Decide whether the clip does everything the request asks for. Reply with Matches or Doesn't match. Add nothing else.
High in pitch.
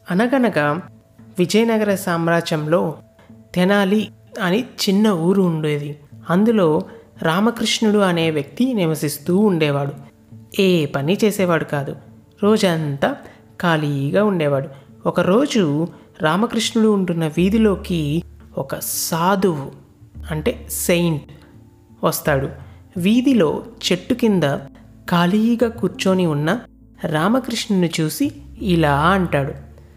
Doesn't match